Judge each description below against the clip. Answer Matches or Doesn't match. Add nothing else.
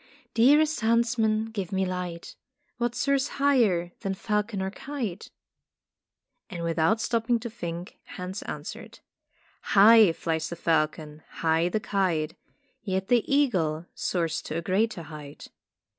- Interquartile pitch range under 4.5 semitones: Doesn't match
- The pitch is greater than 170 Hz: Matches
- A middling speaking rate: Doesn't match